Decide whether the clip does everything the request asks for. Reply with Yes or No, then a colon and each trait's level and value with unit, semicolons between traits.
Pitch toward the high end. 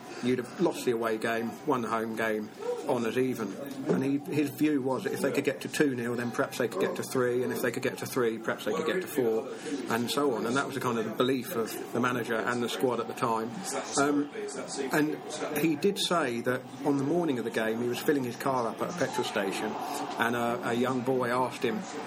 No: low, 130 Hz